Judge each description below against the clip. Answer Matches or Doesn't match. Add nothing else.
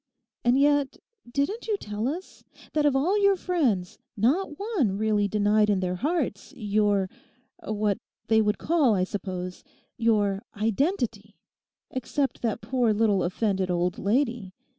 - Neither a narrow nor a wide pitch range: Doesn't match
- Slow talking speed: Matches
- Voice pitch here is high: Matches